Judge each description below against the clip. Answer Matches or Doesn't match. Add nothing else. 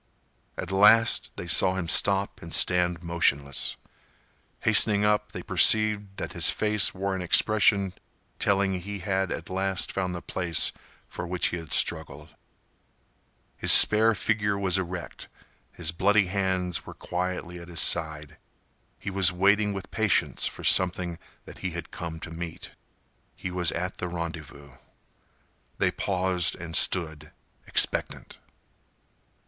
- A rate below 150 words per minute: Matches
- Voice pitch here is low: Matches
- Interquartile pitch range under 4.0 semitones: Matches